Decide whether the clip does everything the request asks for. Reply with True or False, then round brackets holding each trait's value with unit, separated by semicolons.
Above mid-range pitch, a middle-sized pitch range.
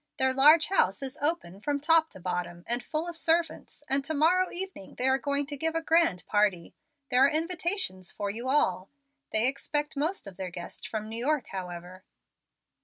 False (270 Hz; 8.5 semitones)